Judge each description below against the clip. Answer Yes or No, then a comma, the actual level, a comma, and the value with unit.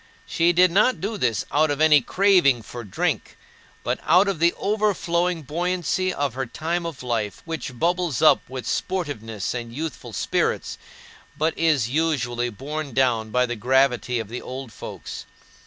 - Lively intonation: Yes, wide, 5.9 semitones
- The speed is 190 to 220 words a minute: No, average, 160 wpm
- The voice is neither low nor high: Yes, medium, 145 Hz